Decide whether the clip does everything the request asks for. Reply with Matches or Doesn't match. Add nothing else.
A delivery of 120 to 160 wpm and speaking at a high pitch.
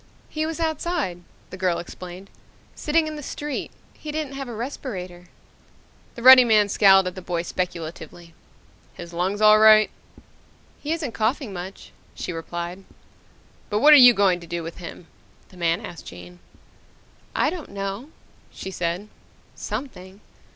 Matches